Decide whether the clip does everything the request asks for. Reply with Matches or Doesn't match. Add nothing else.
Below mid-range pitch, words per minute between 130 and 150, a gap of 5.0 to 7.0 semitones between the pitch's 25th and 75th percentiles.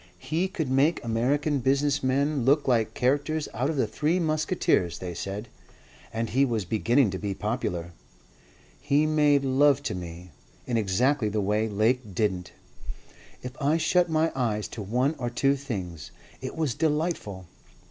Doesn't match